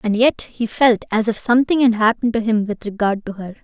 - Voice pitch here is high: Yes, high, 225 Hz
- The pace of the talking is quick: Yes, fast, 250 wpm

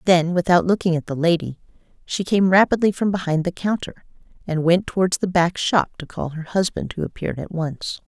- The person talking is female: Yes, female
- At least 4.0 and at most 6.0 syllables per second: Yes, 5.5 syllables/s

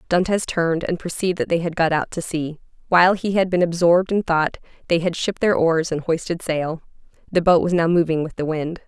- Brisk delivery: Yes, fast, 230 wpm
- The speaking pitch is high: No, medium, 170 Hz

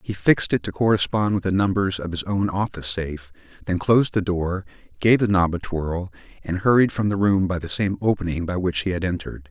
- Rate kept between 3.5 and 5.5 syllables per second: No, 5.9 syllables/s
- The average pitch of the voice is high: No, very low, 95 Hz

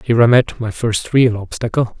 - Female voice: No, male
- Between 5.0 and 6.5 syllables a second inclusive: Yes, 5.1 syllables/s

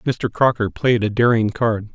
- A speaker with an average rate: Yes, average, 185 wpm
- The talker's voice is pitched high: No, low, 115 Hz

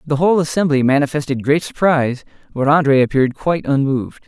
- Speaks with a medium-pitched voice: Yes, medium, 145 Hz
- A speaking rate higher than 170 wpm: No, average, 155 wpm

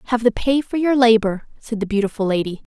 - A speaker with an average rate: No, fast, 215 wpm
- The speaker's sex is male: No, female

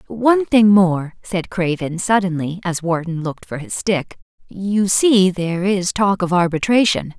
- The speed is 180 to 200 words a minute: No, average, 150 wpm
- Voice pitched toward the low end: No, medium, 185 Hz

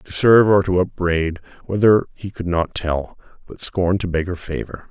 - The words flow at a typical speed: Yes, average, 195 wpm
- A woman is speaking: No, male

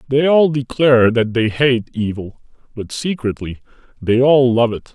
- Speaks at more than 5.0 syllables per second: No, 4.6 syllables/s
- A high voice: No, low, 125 Hz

